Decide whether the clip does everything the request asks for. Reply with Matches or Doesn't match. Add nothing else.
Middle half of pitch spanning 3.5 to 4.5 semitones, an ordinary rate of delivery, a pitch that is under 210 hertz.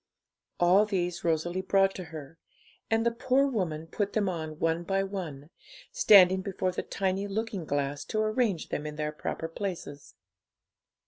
Matches